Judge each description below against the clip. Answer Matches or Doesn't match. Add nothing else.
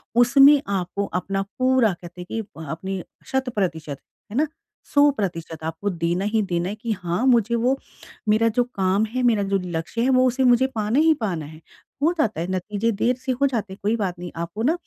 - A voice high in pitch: Matches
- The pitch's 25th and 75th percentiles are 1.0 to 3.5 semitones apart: Doesn't match